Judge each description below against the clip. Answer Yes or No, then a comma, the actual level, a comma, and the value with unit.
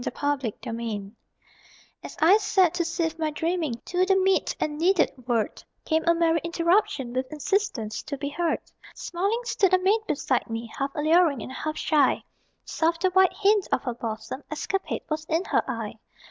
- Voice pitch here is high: Yes, very high, 320 Hz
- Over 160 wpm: Yes, average, 175 wpm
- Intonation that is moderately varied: No, wide, 5.8 semitones